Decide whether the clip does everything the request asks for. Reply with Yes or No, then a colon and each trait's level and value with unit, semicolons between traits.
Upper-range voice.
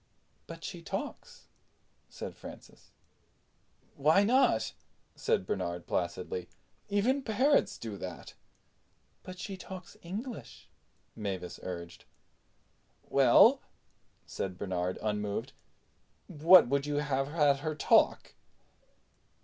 No: medium, 140 Hz